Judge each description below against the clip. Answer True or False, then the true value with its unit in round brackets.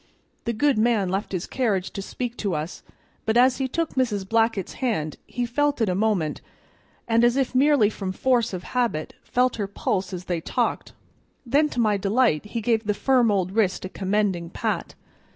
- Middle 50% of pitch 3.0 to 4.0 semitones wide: False (4.5 semitones)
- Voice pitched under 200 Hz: False (220 Hz)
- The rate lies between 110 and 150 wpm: False (190 wpm)